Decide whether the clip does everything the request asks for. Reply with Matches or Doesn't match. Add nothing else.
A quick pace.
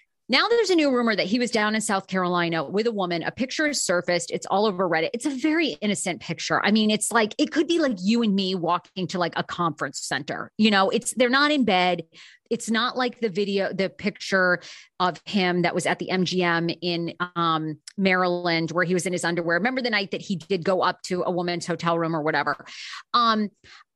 Matches